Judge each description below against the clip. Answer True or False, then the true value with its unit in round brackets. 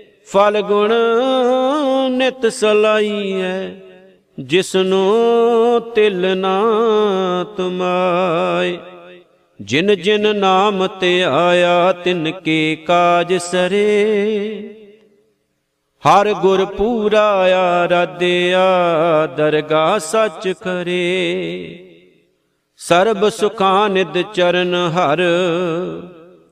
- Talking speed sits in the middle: False (60 wpm)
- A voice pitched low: False (190 Hz)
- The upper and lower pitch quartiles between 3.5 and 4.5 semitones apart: False (3.0 semitones)